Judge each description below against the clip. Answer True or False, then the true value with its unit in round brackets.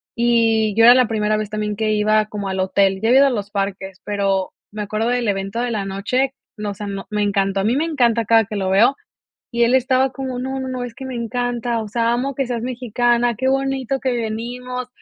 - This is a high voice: True (230 Hz)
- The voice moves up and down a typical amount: True (3.2 semitones)